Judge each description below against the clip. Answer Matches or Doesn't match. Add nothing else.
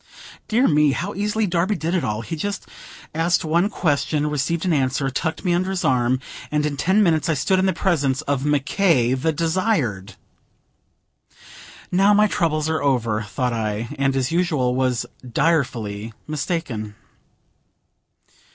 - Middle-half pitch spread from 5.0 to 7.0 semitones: Matches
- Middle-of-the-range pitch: Matches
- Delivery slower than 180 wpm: Matches